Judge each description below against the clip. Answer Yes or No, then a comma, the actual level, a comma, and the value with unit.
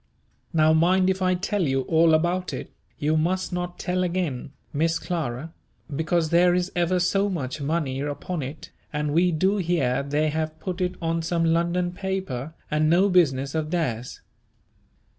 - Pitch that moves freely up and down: No, average, 2.9 semitones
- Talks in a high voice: No, medium, 165 Hz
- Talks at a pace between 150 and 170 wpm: Yes, average, 165 wpm